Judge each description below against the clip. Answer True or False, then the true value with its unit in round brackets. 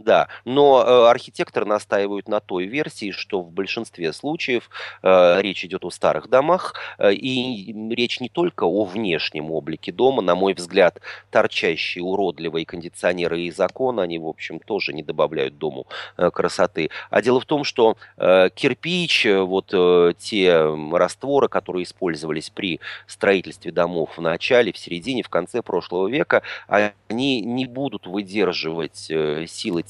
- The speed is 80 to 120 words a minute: False (145 wpm)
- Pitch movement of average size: False (6.1 semitones)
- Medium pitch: False (100 Hz)